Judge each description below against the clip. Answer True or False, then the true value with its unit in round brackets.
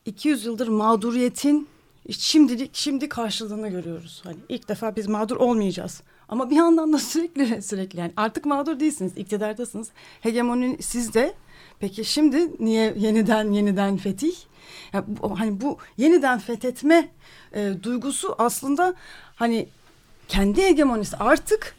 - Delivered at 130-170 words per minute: False (120 wpm)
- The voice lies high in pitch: True (230 Hz)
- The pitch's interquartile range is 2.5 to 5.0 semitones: False (5.5 semitones)